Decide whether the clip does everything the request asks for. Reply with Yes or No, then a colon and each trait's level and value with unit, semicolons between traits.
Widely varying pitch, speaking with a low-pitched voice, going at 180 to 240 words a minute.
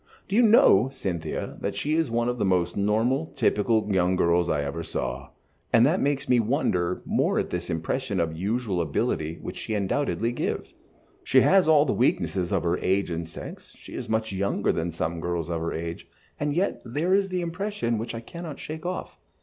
Yes: wide, 8.8 semitones; low, 110 Hz; average, 200 wpm